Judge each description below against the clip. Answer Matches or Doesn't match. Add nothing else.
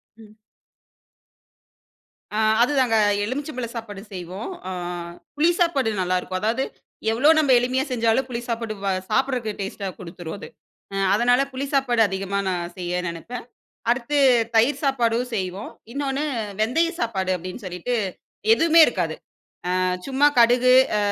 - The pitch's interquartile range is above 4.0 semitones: Matches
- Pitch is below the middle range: Doesn't match